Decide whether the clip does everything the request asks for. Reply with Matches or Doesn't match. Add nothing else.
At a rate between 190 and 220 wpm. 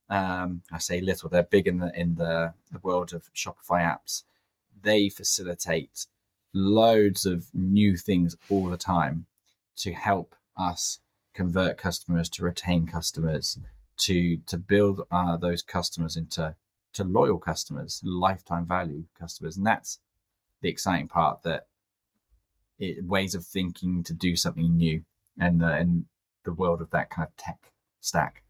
Doesn't match